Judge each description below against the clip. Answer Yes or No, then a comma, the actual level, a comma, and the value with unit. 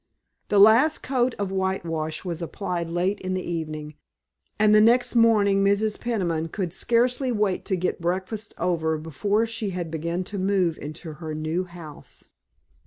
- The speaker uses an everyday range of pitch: Yes, average, 4.2 semitones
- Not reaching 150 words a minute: No, average, 155 wpm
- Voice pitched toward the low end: No, medium, 185 Hz